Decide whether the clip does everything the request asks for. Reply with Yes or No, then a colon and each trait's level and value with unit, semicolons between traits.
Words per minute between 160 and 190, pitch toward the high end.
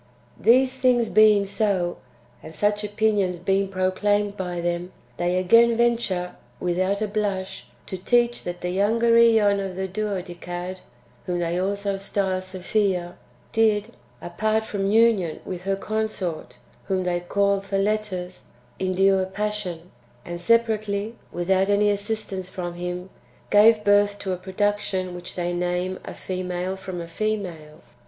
No: average, 140 wpm; high, 195 Hz